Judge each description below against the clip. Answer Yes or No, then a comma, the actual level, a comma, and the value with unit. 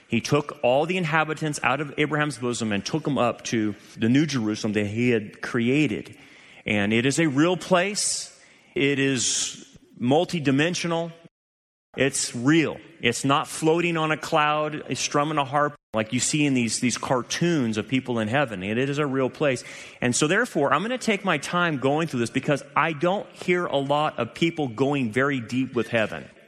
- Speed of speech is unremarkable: Yes, average, 190 wpm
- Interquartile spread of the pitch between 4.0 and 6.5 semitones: Yes, average, 4.5 semitones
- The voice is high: No, medium, 140 Hz